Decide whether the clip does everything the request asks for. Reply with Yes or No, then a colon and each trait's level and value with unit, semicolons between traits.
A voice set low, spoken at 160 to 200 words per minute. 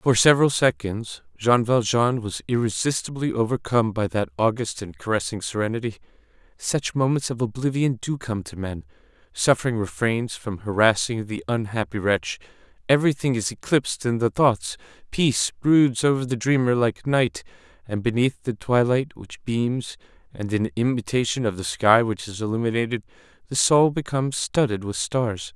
No: low, 115 Hz; average, 150 wpm